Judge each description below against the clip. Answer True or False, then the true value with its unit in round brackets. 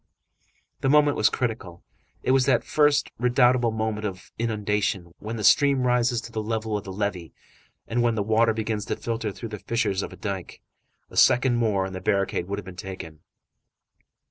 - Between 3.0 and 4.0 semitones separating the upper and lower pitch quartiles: True (3.4 semitones)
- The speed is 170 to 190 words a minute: True (185 wpm)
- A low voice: True (110 Hz)